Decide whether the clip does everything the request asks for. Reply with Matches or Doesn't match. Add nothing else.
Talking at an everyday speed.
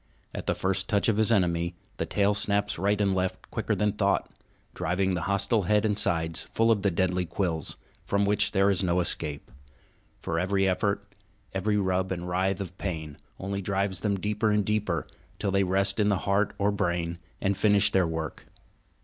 Matches